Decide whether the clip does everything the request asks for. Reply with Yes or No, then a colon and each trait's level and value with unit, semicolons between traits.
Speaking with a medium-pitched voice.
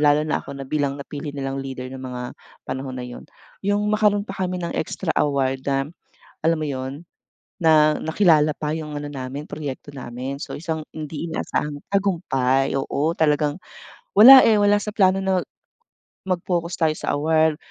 Yes: medium, 150 Hz